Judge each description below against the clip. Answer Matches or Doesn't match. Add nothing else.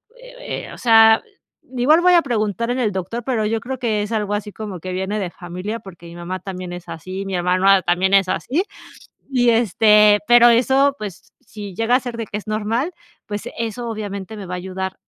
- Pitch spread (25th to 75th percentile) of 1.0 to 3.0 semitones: Doesn't match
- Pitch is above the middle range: Matches